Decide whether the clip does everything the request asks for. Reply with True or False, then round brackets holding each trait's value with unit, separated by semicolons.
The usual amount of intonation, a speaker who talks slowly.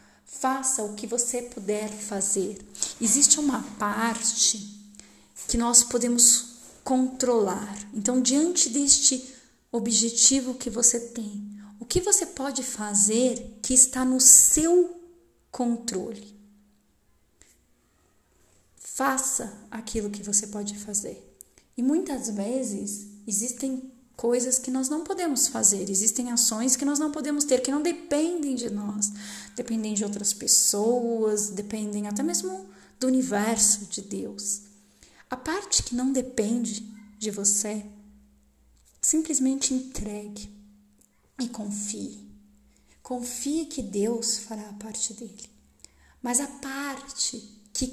True (3.9 semitones; 115 wpm)